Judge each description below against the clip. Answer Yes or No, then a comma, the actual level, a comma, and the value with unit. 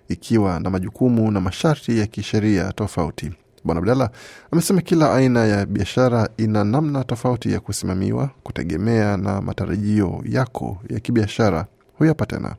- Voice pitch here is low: Yes, low, 110 Hz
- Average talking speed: Yes, average, 130 wpm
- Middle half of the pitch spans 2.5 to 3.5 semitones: No, average, 3.9 semitones